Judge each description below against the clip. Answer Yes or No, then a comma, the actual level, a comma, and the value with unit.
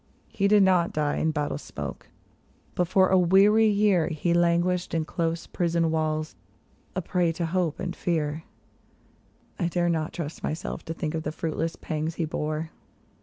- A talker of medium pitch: Yes, medium, 170 Hz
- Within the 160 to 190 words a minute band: Yes, average, 170 wpm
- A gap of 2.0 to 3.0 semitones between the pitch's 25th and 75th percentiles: Yes, narrow, 2.4 semitones